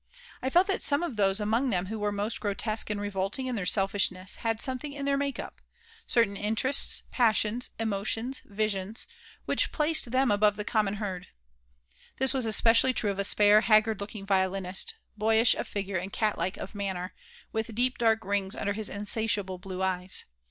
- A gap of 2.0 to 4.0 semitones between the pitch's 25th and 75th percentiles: Yes, average, 2.8 semitones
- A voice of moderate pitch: No, high, 210 Hz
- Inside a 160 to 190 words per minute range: Yes, average, 180 wpm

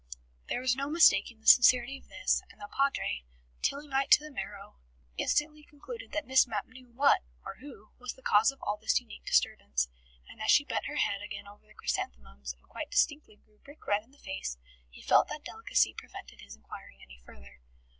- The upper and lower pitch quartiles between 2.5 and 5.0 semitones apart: No, wide, 5.5 semitones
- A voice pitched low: No, high, 240 Hz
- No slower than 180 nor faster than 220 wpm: Yes, average, 200 wpm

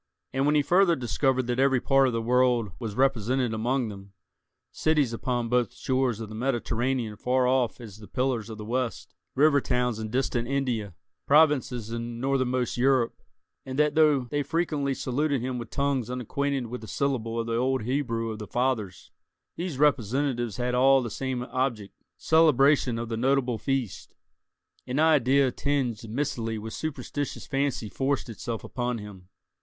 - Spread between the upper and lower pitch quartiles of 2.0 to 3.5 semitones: Yes, average, 2.9 semitones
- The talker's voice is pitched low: Yes, low, 125 Hz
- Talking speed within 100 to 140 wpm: No, average, 160 wpm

